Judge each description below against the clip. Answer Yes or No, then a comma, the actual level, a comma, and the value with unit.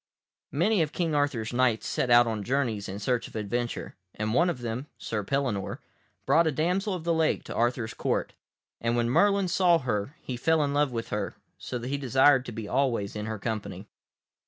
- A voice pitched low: Yes, low, 125 Hz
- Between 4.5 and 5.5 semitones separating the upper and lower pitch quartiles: Yes, average, 5.2 semitones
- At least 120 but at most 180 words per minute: No, fast, 205 wpm